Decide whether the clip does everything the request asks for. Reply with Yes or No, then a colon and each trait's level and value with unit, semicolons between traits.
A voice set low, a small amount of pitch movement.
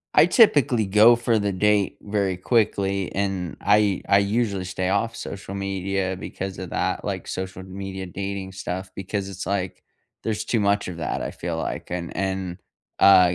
Yes: very low, 95 Hz; narrow, 1.6 semitones